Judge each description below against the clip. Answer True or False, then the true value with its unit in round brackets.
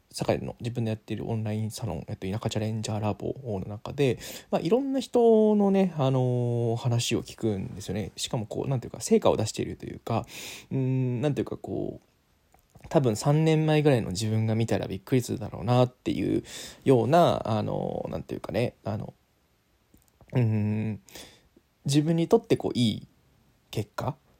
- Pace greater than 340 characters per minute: True (355 characters per minute)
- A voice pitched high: False (120 Hz)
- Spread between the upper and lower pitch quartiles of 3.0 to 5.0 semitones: False (5.5 semitones)